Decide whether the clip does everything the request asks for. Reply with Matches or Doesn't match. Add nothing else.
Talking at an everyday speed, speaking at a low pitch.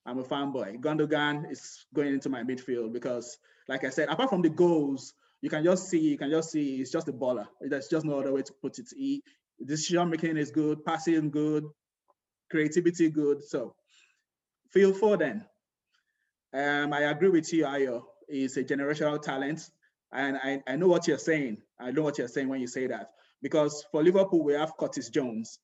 Doesn't match